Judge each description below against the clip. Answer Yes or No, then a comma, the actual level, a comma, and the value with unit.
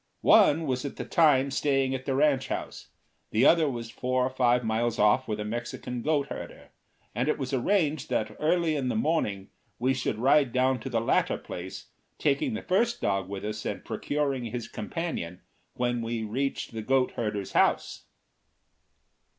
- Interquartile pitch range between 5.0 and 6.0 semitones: No, average, 4.0 semitones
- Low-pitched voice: Yes, low, 130 Hz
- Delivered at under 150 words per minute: No, average, 175 wpm